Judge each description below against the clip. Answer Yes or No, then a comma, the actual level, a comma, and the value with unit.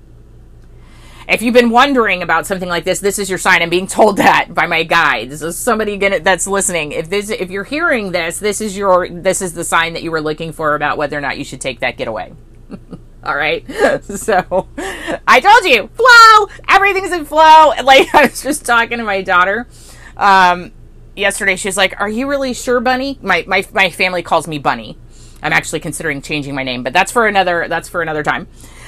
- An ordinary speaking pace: No, fast, 210 wpm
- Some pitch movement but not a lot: No, wide, 5.9 semitones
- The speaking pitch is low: No, medium, 185 Hz